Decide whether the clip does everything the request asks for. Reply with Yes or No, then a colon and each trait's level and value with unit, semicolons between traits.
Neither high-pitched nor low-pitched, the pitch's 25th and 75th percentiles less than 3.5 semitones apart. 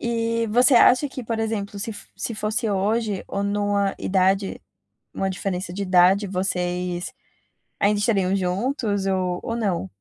No: high, 200 Hz; average, 3.0 semitones